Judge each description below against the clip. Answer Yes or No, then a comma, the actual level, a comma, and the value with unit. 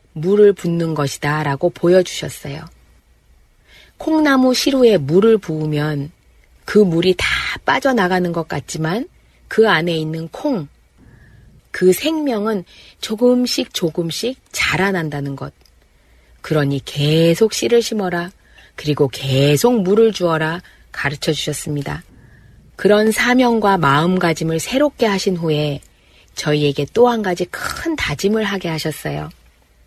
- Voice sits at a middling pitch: Yes, medium, 170 Hz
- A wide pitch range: Yes, wide, 6.8 semitones